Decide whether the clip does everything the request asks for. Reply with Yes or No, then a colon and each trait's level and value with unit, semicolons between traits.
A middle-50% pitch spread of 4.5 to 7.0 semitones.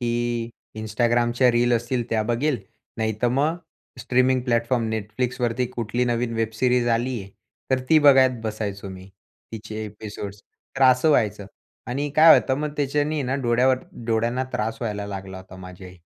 No: average, 2.8 semitones